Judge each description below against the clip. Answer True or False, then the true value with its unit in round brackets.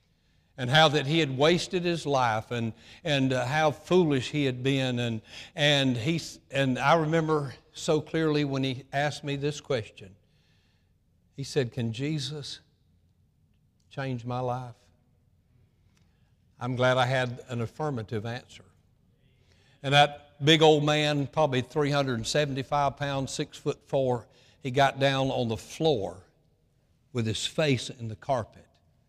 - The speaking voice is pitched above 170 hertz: False (135 Hz)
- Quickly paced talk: False (140 wpm)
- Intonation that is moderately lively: True (3.8 semitones)